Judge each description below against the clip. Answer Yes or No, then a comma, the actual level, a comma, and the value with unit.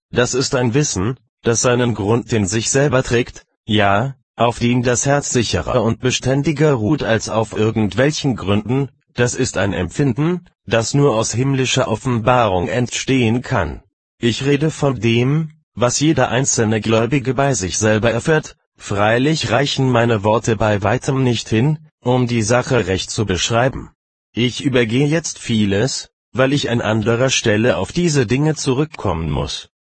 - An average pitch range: Yes, average, 3.5 semitones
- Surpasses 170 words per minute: No, average, 150 wpm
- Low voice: Yes, low, 120 Hz